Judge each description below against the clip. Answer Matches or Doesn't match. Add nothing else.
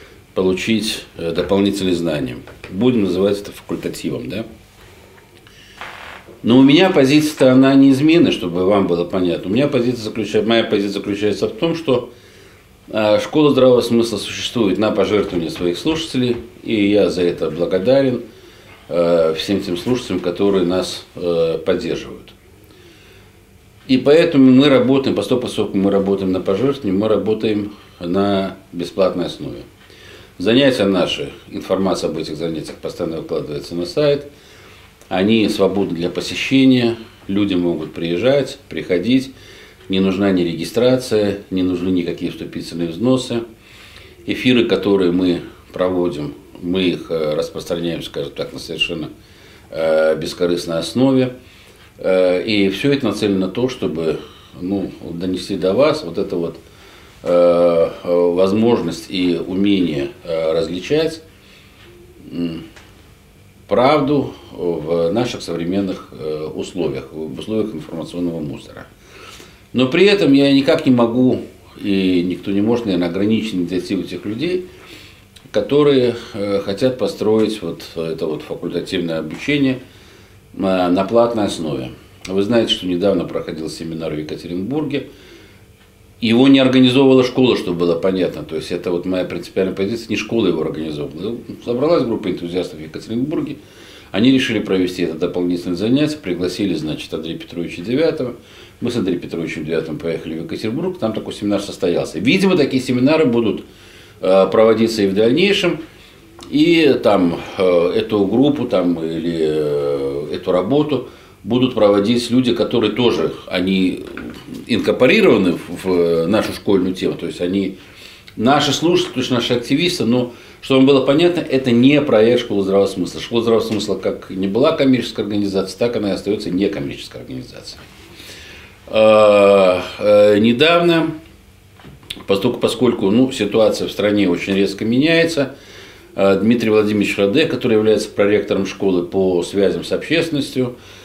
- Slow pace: Doesn't match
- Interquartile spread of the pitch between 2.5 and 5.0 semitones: Doesn't match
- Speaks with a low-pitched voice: Matches